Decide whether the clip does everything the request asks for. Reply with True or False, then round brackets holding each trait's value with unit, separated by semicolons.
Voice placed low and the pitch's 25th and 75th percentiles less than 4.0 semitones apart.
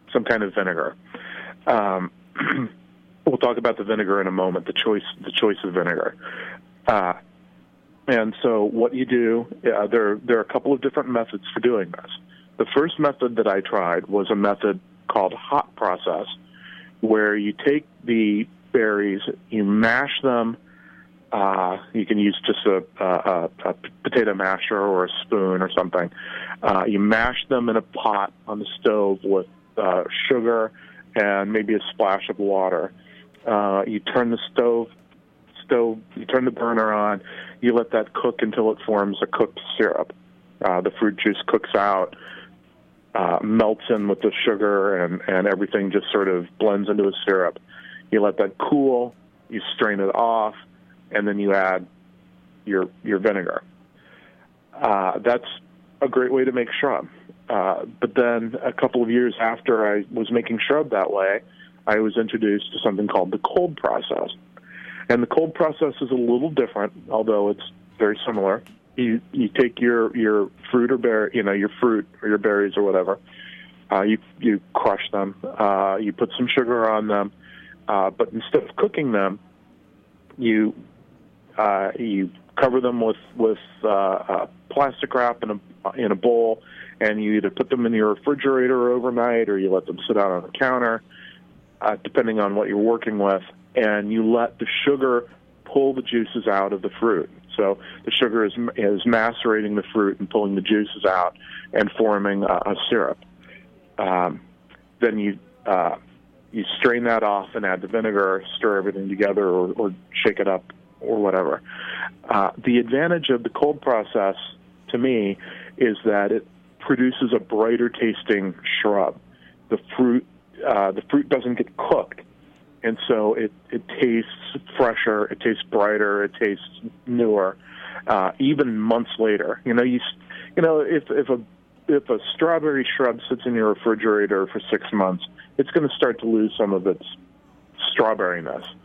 True (105 Hz; 3.3 semitones)